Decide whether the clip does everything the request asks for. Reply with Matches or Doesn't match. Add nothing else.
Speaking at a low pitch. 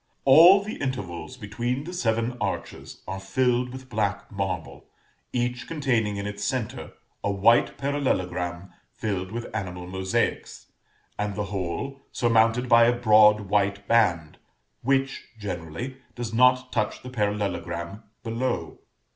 Matches